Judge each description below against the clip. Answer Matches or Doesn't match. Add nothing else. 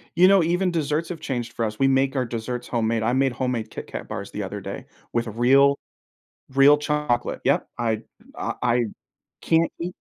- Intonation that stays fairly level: Doesn't match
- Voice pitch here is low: Matches